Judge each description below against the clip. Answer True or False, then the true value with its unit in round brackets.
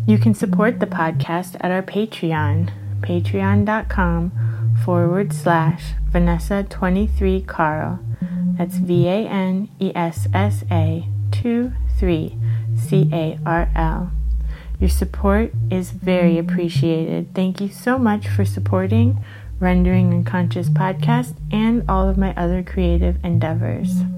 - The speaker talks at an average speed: False (115 wpm)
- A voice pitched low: False (155 Hz)